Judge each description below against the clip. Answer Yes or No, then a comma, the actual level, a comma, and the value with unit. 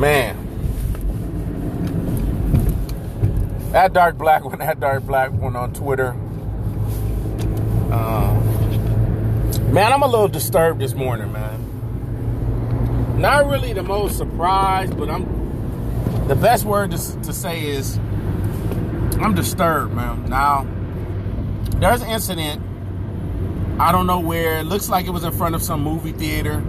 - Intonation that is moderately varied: Yes, average, 3.0 semitones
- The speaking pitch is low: Yes, low, 110 Hz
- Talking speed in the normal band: No, slow, 125 wpm